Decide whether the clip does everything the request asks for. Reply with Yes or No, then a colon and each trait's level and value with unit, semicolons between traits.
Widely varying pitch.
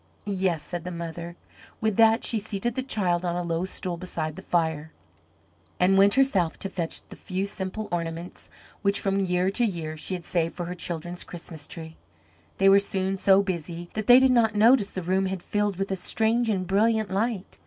No: average, 3.2 semitones